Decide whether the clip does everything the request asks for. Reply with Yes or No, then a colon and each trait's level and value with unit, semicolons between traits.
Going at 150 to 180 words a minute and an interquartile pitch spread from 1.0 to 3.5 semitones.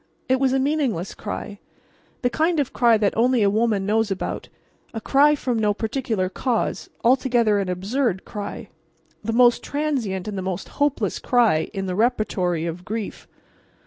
No: average, 165 wpm; average, 4.5 semitones